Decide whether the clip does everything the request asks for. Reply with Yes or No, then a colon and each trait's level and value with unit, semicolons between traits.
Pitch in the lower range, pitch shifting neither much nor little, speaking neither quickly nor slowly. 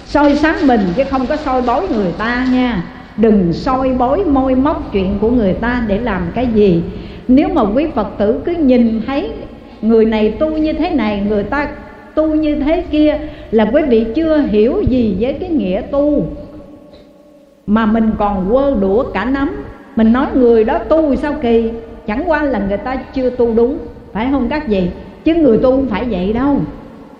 No: very high, 255 Hz; average, 4.7 semitones; average, 190 wpm